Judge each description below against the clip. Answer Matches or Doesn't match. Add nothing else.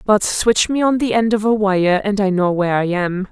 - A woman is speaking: Matches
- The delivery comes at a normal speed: Doesn't match